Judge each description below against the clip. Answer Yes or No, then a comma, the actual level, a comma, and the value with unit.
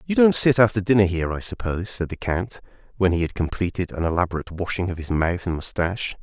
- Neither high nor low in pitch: No, very low, 95 Hz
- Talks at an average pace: No, fast, 220 wpm